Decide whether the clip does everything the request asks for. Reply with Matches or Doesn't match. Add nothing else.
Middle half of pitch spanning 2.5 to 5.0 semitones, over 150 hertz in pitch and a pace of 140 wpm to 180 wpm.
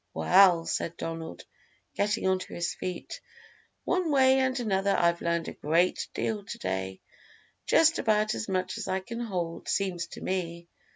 Matches